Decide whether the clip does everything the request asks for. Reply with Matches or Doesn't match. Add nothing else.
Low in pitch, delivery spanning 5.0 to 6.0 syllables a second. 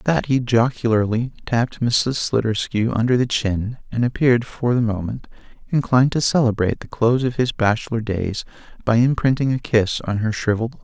Matches